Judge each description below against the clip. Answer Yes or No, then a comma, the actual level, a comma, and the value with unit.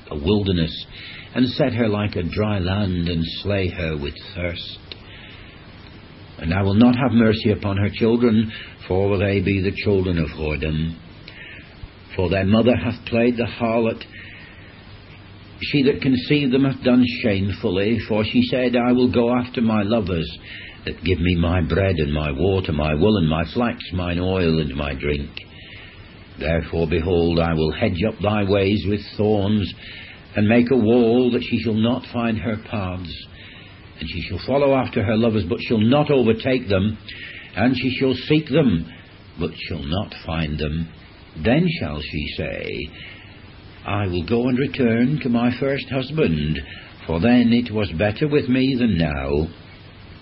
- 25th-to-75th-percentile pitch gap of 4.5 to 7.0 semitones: Yes, average, 5.2 semitones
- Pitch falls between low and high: No, low, 100 Hz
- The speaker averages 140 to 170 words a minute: Yes, average, 165 wpm